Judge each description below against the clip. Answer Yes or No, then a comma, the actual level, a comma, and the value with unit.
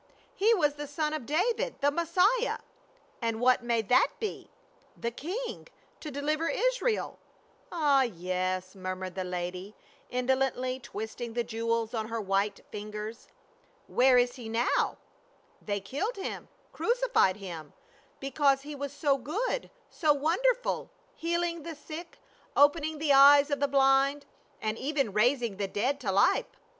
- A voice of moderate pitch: No, very high, 270 Hz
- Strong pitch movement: Yes, wide, 5.8 semitones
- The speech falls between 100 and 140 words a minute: No, average, 155 wpm